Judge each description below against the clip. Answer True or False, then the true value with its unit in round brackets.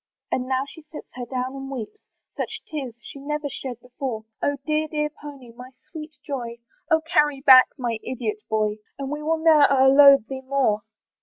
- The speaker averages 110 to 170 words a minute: False (180 wpm)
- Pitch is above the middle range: True (270 Hz)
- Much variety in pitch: False (3.2 semitones)